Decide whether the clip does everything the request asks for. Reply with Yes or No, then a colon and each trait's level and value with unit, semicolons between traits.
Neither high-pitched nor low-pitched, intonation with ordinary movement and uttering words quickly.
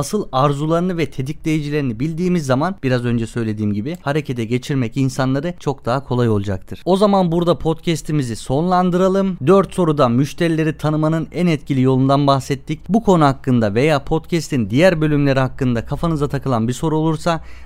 Yes: medium, 145 Hz; average, 4.2 semitones; fast, 145 wpm